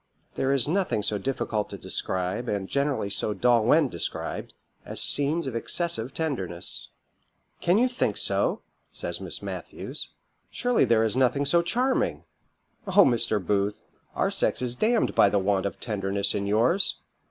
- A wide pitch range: Yes, wide, 7.7 semitones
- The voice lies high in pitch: No, low, 120 Hz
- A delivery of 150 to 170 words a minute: Yes, average, 160 wpm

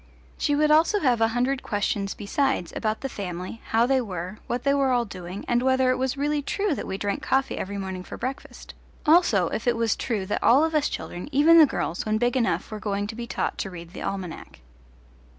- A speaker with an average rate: No, fast, 225 wpm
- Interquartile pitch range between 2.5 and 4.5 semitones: No, average, 5.3 semitones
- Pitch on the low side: No, high, 235 Hz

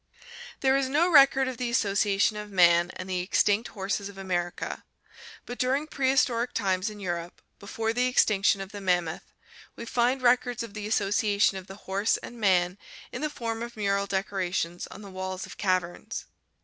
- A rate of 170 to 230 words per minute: Yes, average, 175 wpm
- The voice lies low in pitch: No, high, 205 Hz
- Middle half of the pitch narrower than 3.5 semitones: No, average, 4.1 semitones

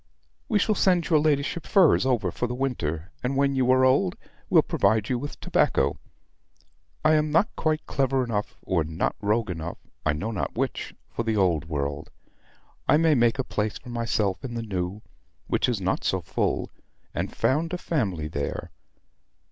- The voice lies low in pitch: Yes, low, 120 Hz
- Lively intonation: Yes, wide, 7.0 semitones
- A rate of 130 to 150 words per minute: No, average, 180 wpm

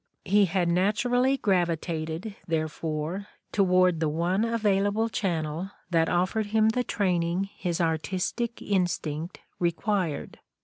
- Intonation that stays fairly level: No, average, 3.7 semitones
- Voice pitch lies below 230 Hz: Yes, medium, 185 Hz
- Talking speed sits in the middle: No, slow, 125 wpm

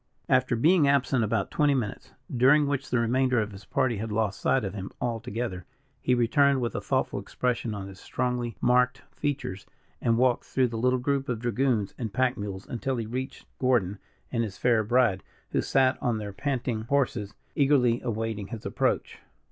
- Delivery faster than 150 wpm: Yes, average, 180 wpm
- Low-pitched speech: Yes, low, 120 Hz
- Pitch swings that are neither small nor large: Yes, average, 3.1 semitones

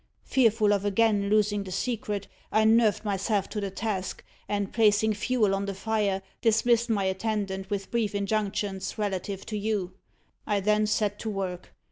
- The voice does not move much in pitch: Yes, narrow, 1.8 semitones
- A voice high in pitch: Yes, high, 205 Hz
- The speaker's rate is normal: Yes, average, 160 wpm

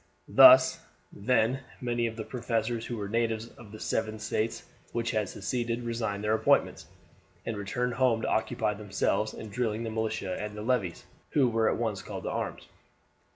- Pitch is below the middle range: Yes, low, 110 Hz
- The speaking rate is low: No, average, 175 wpm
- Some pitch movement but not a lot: No, narrow, 1.8 semitones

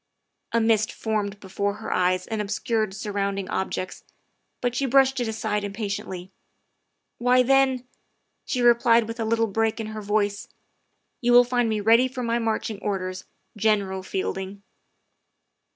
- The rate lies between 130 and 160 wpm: Yes, average, 155 wpm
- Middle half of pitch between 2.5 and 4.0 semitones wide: Yes, average, 2.9 semitones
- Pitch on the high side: Yes, high, 220 Hz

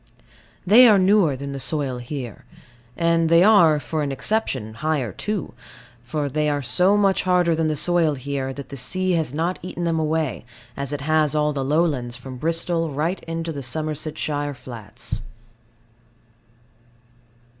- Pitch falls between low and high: Yes, medium, 155 Hz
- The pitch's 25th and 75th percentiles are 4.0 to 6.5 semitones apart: No, average, 3.6 semitones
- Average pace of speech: Yes, average, 155 wpm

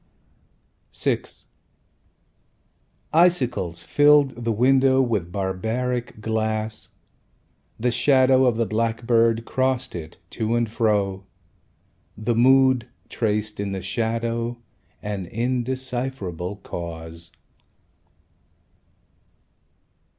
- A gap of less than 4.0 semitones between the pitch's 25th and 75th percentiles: Yes, average, 3.5 semitones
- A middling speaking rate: No, slow, 80 wpm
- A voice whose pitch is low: Yes, low, 115 Hz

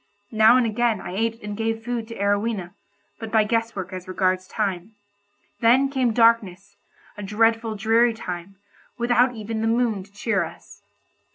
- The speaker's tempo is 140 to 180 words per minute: Yes, average, 165 wpm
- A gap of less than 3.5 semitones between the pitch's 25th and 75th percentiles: Yes, narrow, 2.4 semitones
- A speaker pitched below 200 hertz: No, high, 220 Hz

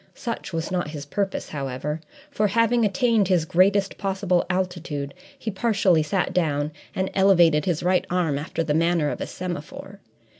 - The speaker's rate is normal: Yes, average, 160 wpm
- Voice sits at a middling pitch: Yes, medium, 180 Hz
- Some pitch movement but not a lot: Yes, average, 4.0 semitones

